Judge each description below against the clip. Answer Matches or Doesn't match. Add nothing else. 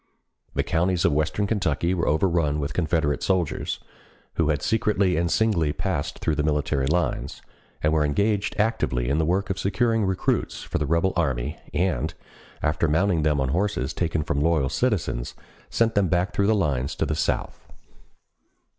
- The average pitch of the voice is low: Matches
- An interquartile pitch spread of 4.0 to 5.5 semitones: Matches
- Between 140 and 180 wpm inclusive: Matches